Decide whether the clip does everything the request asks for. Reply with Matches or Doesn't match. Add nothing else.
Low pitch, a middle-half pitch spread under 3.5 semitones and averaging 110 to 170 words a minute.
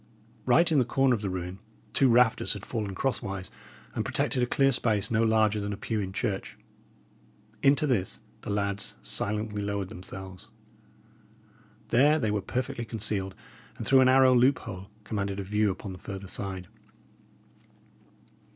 Doesn't match